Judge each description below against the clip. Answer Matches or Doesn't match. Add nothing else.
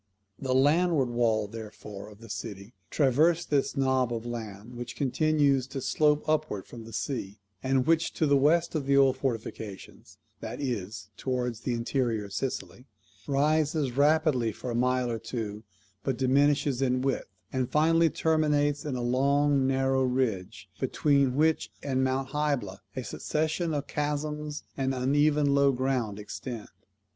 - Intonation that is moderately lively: Matches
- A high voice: Doesn't match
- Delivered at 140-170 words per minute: Matches